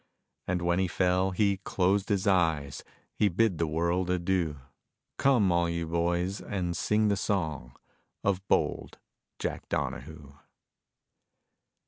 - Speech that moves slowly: Yes, slow, 125 wpm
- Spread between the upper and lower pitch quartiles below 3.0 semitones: Yes, narrow, 2.5 semitones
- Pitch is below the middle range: Yes, very low, 90 Hz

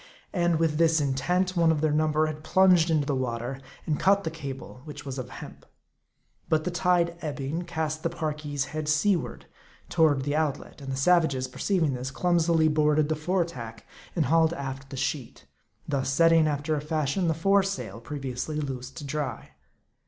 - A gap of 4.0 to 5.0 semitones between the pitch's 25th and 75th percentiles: No, average, 3.3 semitones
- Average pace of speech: Yes, average, 180 wpm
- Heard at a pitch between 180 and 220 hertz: No, medium, 155 Hz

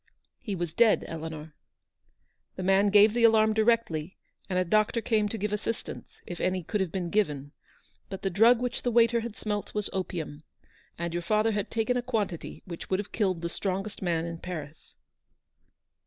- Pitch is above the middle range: Yes, high, 195 Hz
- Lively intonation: No, average, 4.2 semitones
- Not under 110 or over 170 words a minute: No, average, 185 wpm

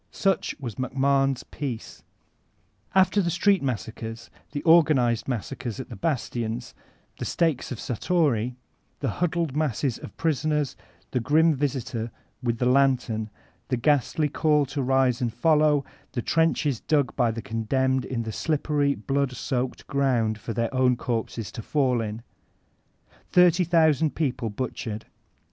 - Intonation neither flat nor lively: Yes, average, 4.1 semitones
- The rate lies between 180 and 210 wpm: No, average, 140 wpm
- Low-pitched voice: Yes, low, 130 Hz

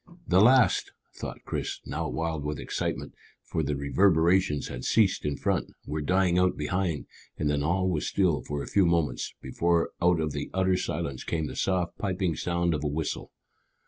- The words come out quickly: No, average, 180 wpm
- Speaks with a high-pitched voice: No, very low, 85 Hz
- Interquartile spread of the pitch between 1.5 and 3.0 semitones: No, average, 3.8 semitones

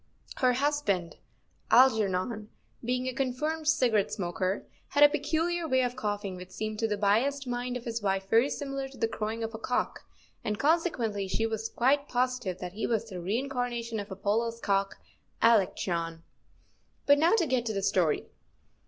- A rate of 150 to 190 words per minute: Yes, average, 170 wpm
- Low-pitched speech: No, high, 230 Hz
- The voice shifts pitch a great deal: No, average, 4.4 semitones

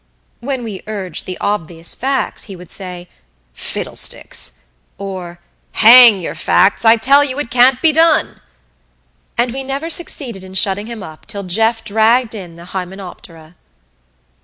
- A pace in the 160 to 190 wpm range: No, average, 145 wpm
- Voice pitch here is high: Yes, high, 210 Hz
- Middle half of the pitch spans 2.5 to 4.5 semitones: No, wide, 5.4 semitones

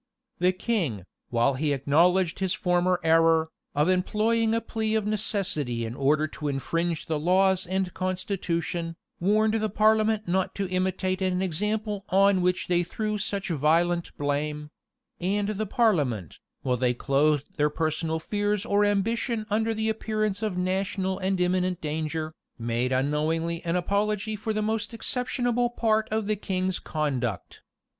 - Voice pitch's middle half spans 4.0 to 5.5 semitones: Yes, average, 5.1 semitones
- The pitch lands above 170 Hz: Yes, medium, 185 Hz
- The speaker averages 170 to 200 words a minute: No, average, 150 wpm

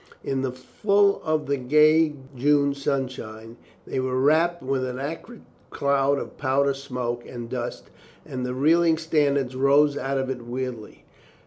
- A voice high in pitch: No, low, 135 Hz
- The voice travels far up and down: No, narrow, 2.6 semitones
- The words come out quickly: No, average, 150 wpm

